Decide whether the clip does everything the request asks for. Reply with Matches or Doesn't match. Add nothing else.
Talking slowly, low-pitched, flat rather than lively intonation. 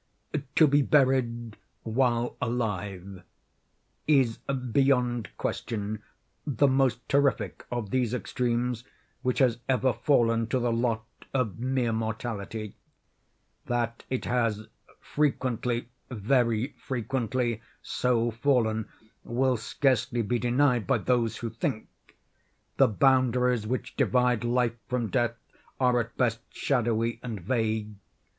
Matches